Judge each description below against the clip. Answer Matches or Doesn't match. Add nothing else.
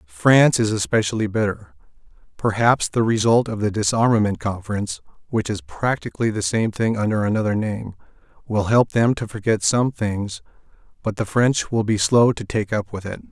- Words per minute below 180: Matches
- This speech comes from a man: Matches